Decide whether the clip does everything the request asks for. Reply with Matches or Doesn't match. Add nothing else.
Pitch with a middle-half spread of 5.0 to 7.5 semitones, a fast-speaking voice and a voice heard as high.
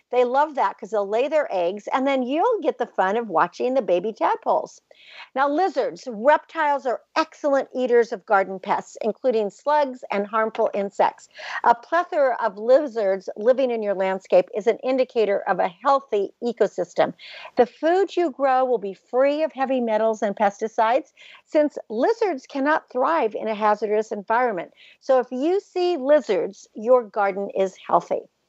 Doesn't match